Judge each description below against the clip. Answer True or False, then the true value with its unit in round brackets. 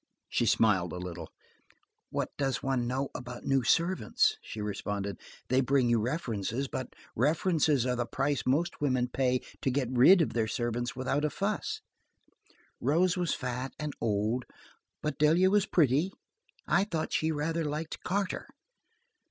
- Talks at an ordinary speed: True (150 wpm)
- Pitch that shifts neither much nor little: True (4.6 semitones)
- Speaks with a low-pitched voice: True (130 Hz)